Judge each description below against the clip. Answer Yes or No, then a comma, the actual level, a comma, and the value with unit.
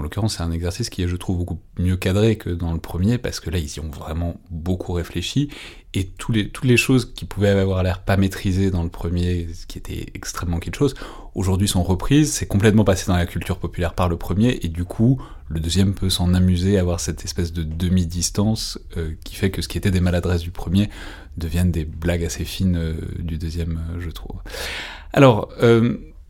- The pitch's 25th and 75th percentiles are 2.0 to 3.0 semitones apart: Yes, average, 2.7 semitones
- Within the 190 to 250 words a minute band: Yes, fast, 220 wpm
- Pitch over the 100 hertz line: No, very low, 90 Hz